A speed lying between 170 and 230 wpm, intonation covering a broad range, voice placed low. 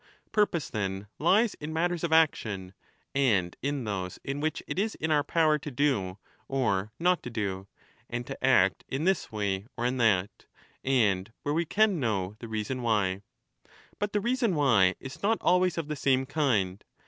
Yes: average, 180 wpm; wide, 7.9 semitones; low, 130 Hz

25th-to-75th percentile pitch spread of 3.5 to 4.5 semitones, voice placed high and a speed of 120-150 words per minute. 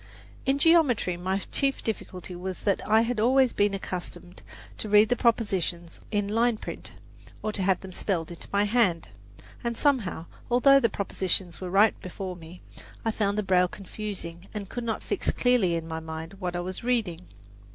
No: average, 4.2 semitones; high, 200 Hz; average, 180 wpm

